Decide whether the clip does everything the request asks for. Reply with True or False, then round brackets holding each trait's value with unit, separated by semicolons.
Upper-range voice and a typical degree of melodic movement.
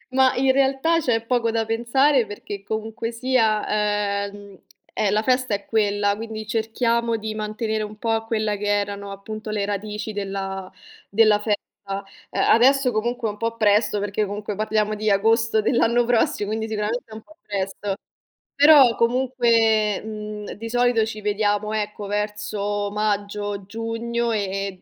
False (215 Hz; 2.0 semitones)